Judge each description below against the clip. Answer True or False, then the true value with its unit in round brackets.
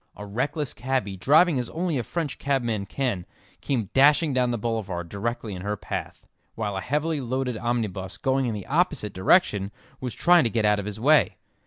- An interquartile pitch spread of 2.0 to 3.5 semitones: False (5.2 semitones)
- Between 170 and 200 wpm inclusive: True (190 wpm)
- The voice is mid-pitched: False (120 Hz)